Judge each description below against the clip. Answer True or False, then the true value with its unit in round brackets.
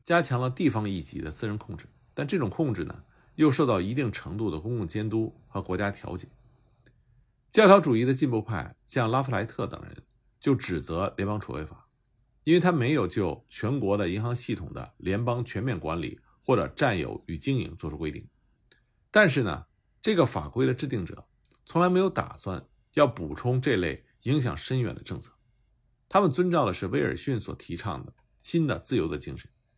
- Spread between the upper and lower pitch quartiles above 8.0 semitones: False (5.3 semitones)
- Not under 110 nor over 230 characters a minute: False (280 characters per minute)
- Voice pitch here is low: True (120 Hz)